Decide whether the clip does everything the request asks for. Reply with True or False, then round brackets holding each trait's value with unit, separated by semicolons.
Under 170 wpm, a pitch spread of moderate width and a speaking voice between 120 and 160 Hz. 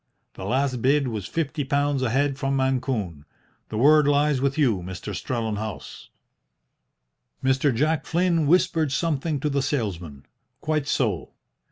True (140 wpm; 4.7 semitones; 135 Hz)